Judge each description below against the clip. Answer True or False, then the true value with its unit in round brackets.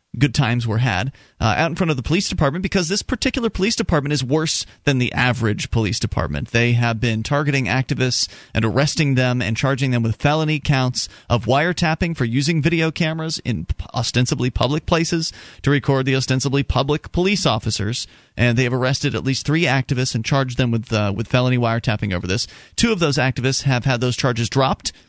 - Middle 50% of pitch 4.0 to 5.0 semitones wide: True (4.3 semitones)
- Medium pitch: False (130 Hz)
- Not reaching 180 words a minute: False (195 wpm)